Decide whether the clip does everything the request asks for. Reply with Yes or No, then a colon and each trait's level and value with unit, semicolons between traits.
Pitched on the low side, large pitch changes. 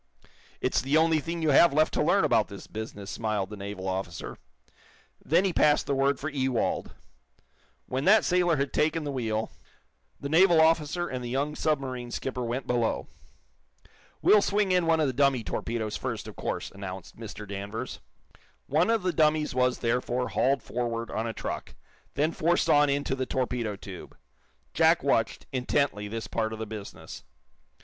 Yes: low, 130 Hz; wide, 5.7 semitones